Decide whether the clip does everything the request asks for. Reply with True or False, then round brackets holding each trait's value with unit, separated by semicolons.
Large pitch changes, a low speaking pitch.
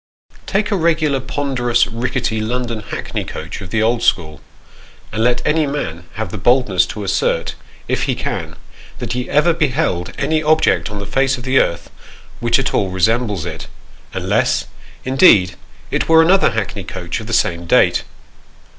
True (5.8 semitones; 120 Hz)